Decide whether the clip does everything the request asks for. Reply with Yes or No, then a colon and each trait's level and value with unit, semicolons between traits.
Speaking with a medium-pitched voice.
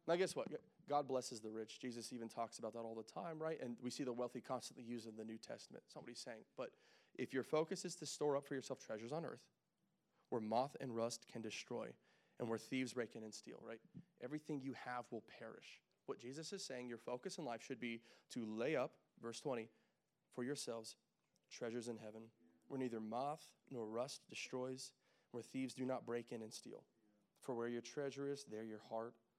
No: low, 125 Hz